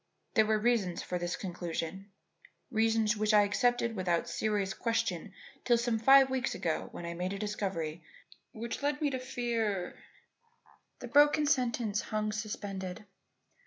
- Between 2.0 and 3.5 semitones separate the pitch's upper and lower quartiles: No, average, 4.1 semitones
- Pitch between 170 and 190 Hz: No, high, 215 Hz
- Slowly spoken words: No, average, 150 wpm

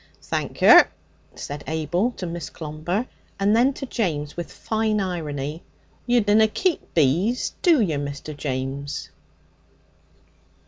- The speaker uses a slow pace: Yes, slow, 125 wpm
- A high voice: No, medium, 175 Hz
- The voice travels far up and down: Yes, wide, 6.8 semitones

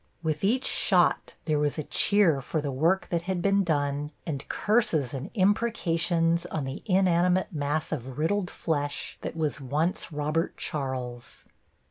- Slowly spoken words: No, average, 150 wpm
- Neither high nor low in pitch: Yes, medium, 160 Hz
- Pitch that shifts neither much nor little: Yes, average, 4.1 semitones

